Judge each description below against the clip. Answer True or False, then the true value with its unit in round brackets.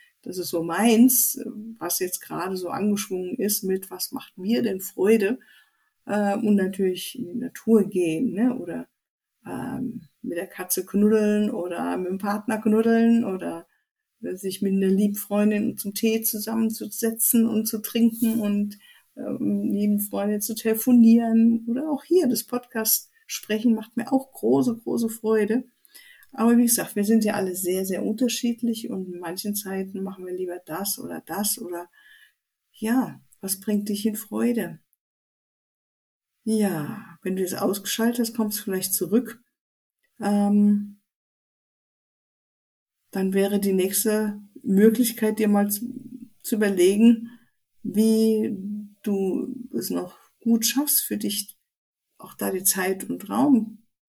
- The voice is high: True (215 Hz)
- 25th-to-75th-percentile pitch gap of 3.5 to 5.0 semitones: False (3.1 semitones)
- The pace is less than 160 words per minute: True (135 wpm)